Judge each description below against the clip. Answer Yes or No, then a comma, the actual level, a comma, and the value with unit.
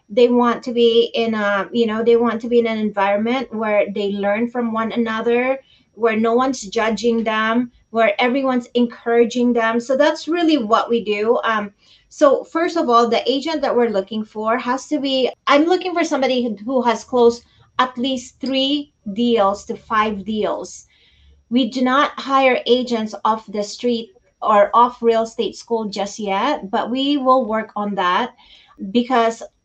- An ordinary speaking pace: Yes, average, 175 wpm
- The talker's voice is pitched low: No, high, 235 Hz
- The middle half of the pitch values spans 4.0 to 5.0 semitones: No, average, 2.7 semitones